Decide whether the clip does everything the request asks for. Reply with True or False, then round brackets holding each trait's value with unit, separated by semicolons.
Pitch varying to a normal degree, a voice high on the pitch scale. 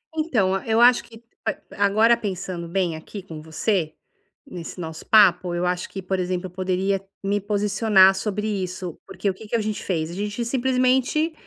True (3.3 semitones; 195 Hz)